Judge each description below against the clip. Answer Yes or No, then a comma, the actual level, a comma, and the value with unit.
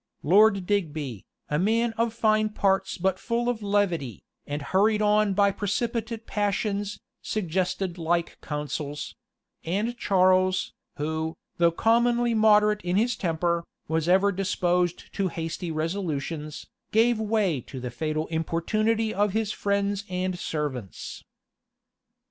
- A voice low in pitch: No, high, 190 Hz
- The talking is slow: Yes, slow, 125 wpm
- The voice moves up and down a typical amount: Yes, average, 4.5 semitones